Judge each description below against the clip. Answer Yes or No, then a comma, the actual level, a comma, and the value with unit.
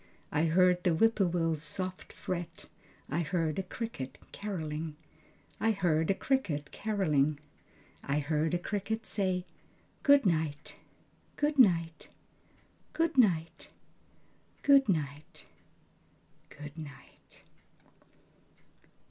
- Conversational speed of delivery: No, slow, 95 wpm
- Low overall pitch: No, medium, 175 Hz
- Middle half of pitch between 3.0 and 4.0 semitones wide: No, average, 4.7 semitones